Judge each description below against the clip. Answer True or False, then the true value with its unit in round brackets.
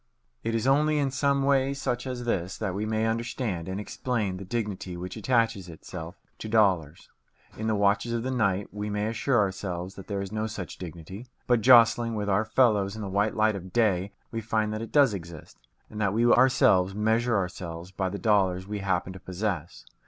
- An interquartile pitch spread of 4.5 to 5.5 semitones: False (3.6 semitones)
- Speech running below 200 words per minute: False (205 wpm)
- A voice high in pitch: False (105 Hz)